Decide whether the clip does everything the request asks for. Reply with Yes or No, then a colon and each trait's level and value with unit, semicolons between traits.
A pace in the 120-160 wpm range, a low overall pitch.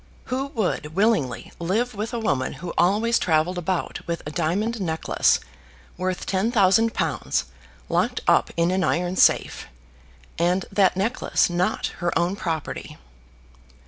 No: average, 140 wpm; medium, 185 Hz